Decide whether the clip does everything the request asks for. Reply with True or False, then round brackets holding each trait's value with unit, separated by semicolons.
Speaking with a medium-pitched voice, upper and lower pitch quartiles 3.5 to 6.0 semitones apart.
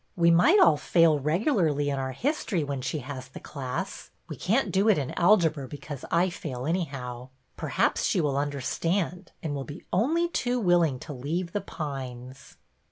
True (155 Hz; 4.8 semitones)